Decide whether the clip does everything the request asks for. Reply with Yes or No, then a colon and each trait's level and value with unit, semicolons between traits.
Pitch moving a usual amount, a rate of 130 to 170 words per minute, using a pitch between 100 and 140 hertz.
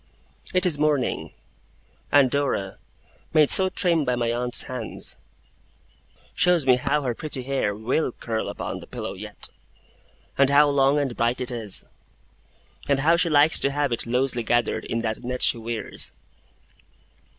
Yes: average, 3.5 semitones; average, 155 wpm; low, 135 Hz